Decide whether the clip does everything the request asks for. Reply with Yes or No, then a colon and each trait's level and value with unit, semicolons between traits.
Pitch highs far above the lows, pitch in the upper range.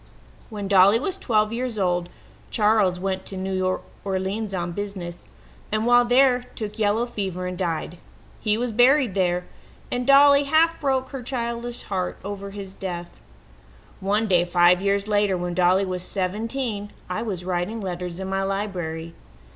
No: average, 4.0 semitones; high, 200 Hz